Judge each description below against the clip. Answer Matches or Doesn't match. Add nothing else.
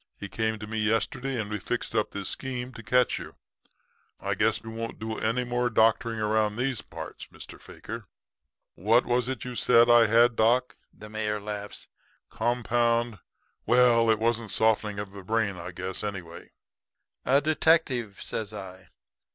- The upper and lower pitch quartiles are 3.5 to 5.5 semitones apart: Doesn't match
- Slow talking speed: Doesn't match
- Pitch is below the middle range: Matches